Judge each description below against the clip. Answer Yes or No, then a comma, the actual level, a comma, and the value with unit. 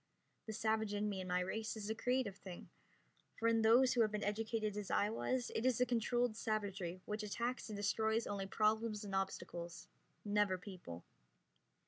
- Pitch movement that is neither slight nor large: No, narrow, 2.2 semitones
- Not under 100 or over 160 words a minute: No, average, 180 wpm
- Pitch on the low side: No, high, 215 Hz